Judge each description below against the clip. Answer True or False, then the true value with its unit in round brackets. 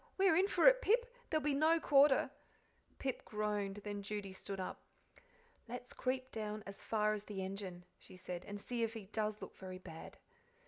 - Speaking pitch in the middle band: False (215 Hz)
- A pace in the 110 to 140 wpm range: False (190 wpm)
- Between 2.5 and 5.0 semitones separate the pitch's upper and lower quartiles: False (5.5 semitones)